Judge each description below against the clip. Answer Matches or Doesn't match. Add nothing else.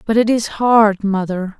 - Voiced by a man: Doesn't match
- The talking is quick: Doesn't match